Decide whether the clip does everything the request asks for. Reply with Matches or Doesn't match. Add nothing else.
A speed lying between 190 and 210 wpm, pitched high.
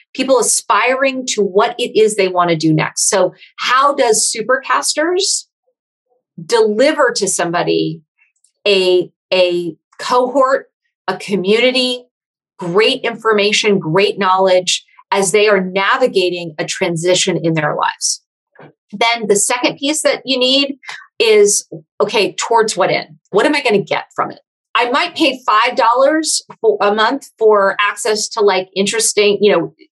Doesn't match